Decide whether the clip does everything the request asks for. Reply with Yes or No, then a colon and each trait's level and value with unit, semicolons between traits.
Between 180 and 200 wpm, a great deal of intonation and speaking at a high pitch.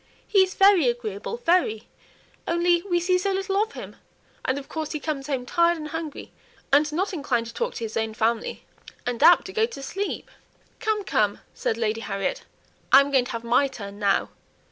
Yes: average, 195 wpm; wide, 7.7 semitones; very high, 290 Hz